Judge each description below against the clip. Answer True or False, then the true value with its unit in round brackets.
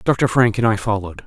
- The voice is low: True (110 Hz)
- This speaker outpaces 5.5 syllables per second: True (6.0 syllables/s)